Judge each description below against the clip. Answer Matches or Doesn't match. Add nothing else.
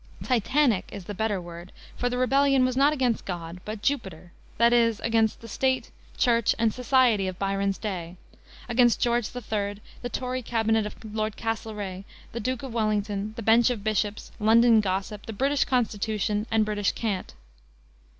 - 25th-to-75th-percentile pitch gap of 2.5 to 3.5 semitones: Matches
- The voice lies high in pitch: Matches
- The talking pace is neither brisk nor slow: Matches